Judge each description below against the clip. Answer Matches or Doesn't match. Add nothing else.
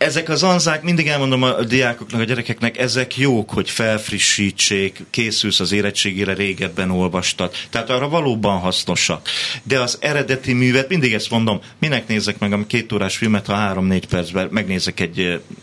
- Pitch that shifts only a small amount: Doesn't match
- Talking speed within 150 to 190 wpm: Matches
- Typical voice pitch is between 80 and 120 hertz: Matches